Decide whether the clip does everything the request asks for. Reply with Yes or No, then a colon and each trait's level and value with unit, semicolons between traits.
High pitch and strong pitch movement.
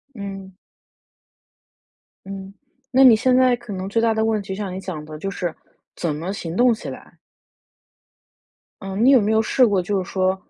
No: high, 200 Hz; average, 3.2 semitones